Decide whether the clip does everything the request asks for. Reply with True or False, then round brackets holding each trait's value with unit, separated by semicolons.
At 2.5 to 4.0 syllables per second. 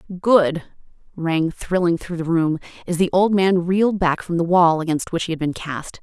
False (4.9 syllables/s)